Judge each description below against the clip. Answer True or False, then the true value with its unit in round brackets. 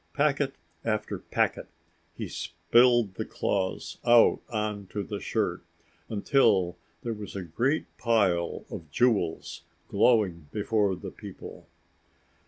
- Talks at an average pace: False (115 wpm)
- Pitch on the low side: True (105 Hz)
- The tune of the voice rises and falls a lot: False (4.2 semitones)